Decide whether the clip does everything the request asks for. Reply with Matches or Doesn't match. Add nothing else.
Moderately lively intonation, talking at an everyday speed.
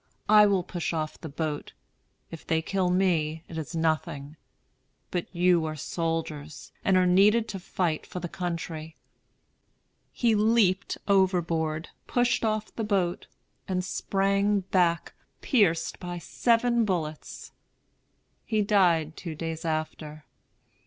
Doesn't match